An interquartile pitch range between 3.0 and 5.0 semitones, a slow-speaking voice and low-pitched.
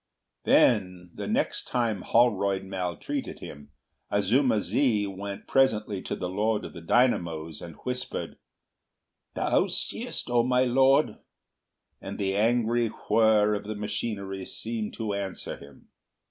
Yes: average, 3.6 semitones; slow, 130 wpm; low, 105 Hz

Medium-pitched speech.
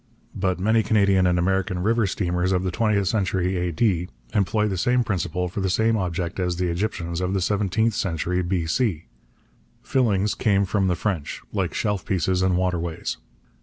No: very low, 95 Hz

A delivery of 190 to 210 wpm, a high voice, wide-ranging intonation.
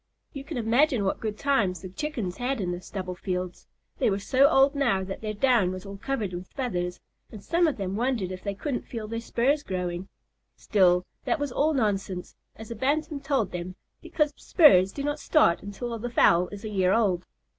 Yes: fast, 205 wpm; high, 215 Hz; wide, 6.6 semitones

